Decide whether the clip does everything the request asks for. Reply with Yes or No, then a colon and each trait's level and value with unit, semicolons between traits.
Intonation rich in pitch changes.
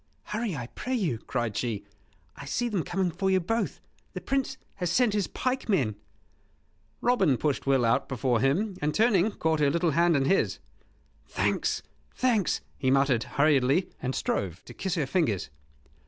Yes: wide, 7.2 semitones